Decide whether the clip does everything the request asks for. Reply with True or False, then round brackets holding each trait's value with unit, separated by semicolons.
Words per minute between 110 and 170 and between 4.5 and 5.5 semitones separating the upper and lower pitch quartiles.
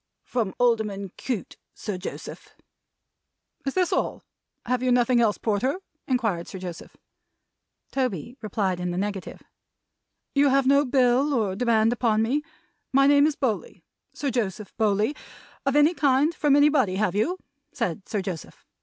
True (145 wpm; 5.1 semitones)